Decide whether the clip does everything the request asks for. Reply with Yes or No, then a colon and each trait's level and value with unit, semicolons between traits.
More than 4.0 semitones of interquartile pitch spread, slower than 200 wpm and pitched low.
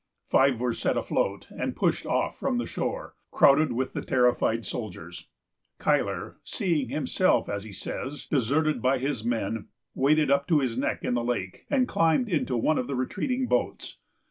Yes: average, 4.7 semitones; average, 170 wpm; low, 130 Hz